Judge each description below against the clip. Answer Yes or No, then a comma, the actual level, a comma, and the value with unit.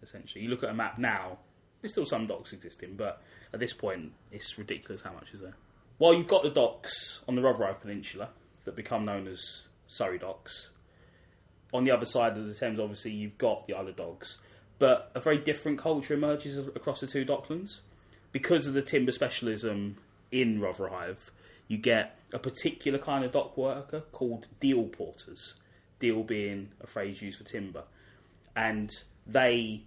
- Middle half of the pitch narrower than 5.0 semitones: No, wide, 5.5 semitones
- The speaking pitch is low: Yes, low, 110 Hz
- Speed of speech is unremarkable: Yes, average, 175 wpm